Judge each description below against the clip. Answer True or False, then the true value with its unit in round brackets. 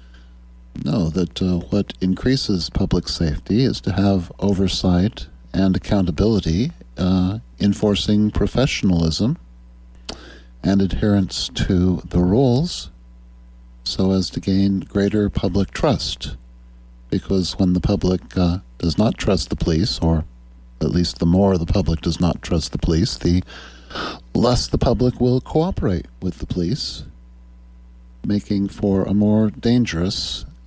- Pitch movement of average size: False (6.2 semitones)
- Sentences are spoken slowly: True (125 wpm)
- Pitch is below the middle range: True (90 Hz)